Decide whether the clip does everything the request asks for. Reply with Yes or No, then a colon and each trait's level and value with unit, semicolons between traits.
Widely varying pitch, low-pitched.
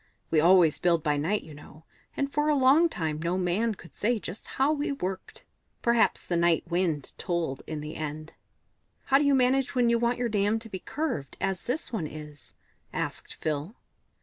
No: wide, 7.7 semitones; medium, 185 Hz